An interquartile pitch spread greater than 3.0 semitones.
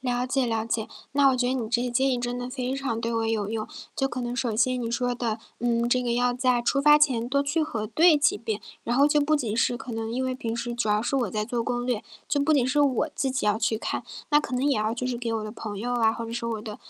No: narrow, 2.5 semitones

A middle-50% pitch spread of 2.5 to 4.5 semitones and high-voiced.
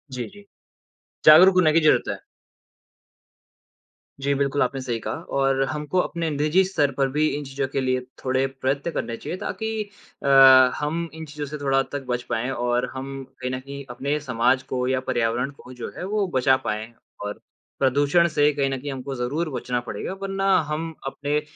No: average, 2.9 semitones; medium, 140 Hz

